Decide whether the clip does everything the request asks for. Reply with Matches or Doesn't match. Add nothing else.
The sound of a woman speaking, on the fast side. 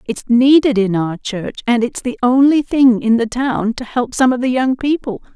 Matches